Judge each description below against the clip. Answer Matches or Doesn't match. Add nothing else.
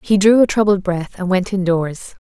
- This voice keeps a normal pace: Doesn't match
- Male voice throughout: Doesn't match